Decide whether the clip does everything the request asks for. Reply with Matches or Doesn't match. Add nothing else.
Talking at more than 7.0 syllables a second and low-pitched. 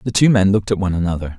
Matches